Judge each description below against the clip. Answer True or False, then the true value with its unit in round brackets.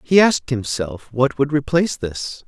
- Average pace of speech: True (170 wpm)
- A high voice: False (140 Hz)